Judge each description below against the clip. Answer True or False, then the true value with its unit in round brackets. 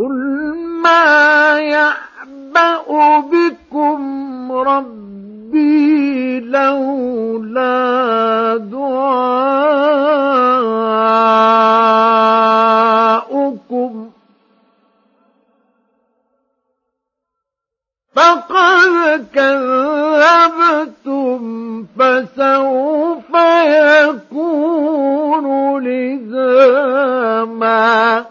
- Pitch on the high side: True (270 Hz)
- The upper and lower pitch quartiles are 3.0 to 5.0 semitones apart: True (4.7 semitones)